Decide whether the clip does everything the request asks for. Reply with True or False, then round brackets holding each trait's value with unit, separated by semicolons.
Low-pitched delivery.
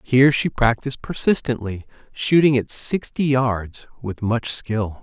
True (125 Hz)